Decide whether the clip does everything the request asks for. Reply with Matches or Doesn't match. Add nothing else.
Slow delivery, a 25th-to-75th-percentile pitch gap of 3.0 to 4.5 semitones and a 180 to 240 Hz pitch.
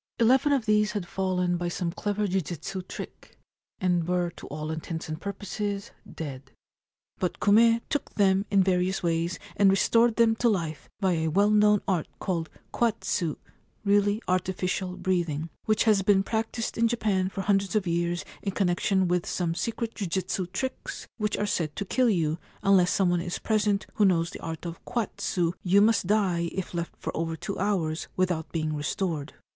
Doesn't match